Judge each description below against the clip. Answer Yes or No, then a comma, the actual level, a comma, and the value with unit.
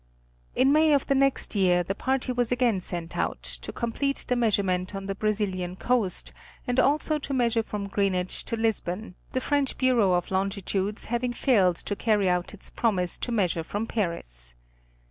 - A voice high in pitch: Yes, high, 210 Hz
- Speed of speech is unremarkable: Yes, average, 175 wpm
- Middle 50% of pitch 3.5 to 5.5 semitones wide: Yes, average, 5.0 semitones